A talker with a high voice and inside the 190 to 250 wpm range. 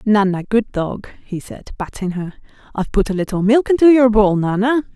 Yes: high, 215 Hz; fast, 205 wpm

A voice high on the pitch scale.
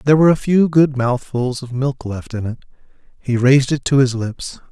No: low, 130 Hz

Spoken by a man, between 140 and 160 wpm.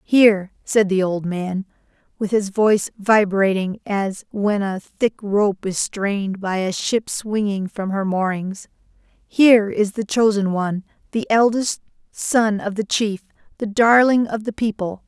No: female; average, 155 wpm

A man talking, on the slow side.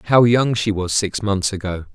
No: male; fast, 215 wpm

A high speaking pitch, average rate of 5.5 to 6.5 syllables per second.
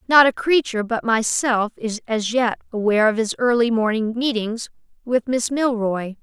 No: high, 230 Hz; 4.8 syllables/s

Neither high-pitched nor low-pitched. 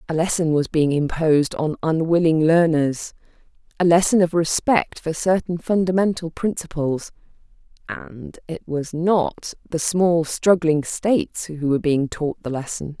Yes: medium, 165 Hz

